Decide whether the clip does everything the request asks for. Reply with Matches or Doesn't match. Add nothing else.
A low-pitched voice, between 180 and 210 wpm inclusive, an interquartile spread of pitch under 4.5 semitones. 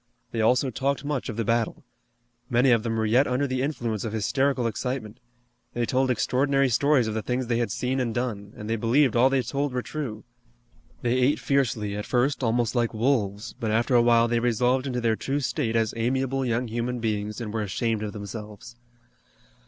Matches